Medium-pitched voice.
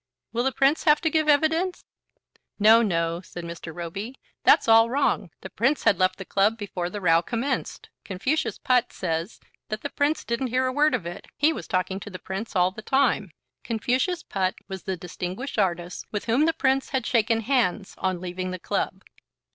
No: high, 220 Hz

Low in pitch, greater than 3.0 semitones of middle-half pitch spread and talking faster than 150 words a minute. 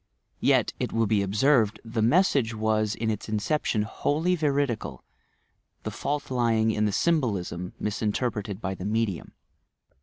No: low, 110 Hz; average, 3.5 semitones; average, 145 wpm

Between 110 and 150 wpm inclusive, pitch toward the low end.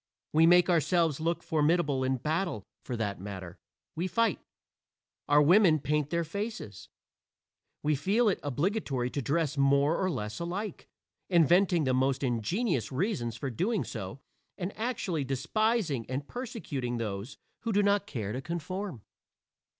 No: average, 140 wpm; medium, 155 Hz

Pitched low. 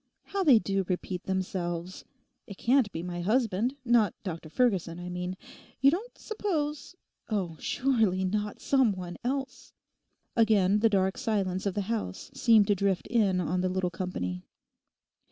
No: high, 200 Hz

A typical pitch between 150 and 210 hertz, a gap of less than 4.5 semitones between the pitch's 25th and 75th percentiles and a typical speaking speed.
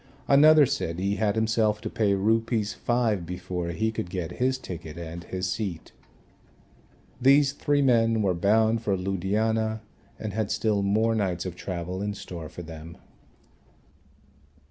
No: low, 105 Hz; average, 3.9 semitones; average, 145 wpm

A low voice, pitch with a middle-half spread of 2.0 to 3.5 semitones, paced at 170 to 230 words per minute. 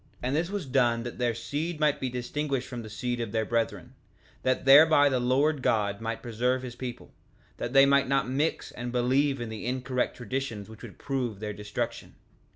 Yes: low, 125 Hz; average, 2.8 semitones; average, 195 wpm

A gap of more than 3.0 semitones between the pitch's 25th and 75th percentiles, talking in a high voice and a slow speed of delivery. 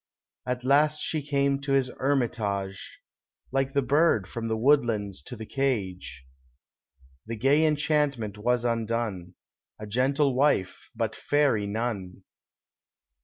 No: average, 4.8 semitones; low, 120 Hz; slow, 120 wpm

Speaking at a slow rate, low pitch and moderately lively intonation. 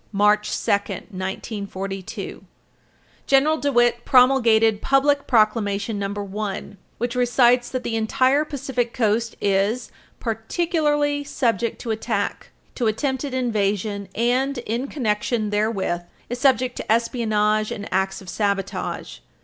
No: slow, 120 wpm; high, 230 Hz; average, 3.7 semitones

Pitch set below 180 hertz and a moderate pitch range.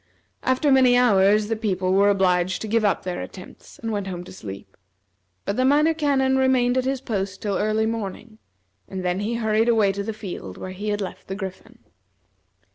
No: high, 210 Hz; average, 4.2 semitones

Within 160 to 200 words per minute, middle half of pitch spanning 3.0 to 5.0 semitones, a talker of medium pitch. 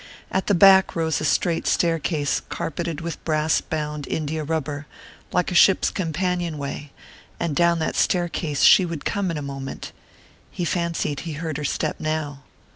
No: average, 165 wpm; narrow, 2.4 semitones; medium, 160 Hz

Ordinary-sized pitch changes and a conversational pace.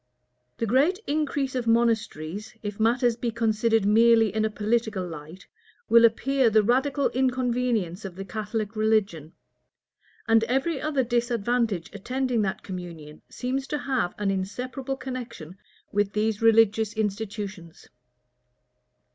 No: average, 3.5 semitones; slow, 125 wpm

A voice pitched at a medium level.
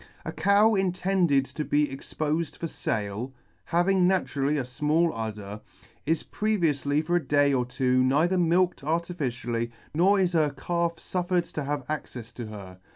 Yes: medium, 150 Hz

